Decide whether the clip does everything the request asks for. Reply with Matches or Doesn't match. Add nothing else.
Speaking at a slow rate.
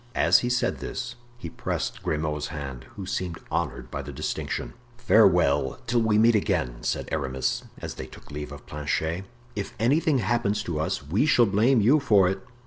Doesn't match